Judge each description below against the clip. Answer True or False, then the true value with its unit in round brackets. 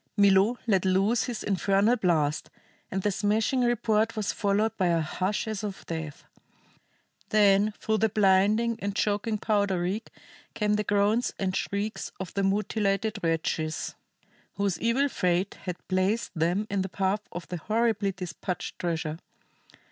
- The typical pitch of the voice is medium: False (200 Hz)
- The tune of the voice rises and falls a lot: False (2.5 semitones)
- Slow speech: False (150 wpm)